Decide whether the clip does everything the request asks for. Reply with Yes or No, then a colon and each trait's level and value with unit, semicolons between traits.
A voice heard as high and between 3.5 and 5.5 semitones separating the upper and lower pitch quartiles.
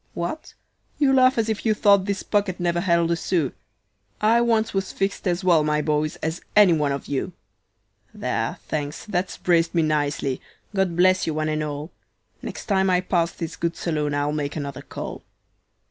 No: medium, 170 Hz; average, 4.2 semitones